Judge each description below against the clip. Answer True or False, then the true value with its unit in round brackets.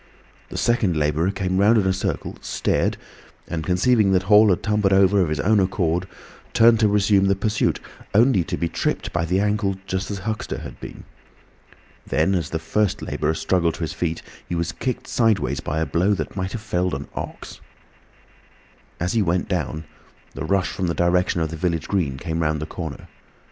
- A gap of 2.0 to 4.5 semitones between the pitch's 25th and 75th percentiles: True (3.5 semitones)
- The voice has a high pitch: False (95 Hz)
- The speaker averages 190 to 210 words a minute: True (195 wpm)